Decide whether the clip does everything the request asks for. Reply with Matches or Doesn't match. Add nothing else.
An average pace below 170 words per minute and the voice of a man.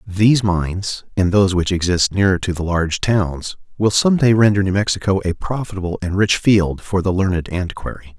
Doesn't match